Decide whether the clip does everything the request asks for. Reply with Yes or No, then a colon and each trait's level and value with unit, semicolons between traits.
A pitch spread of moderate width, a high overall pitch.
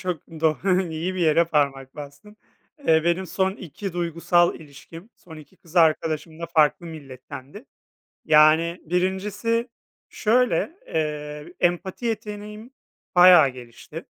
No: average, 3.6 semitones; medium, 170 Hz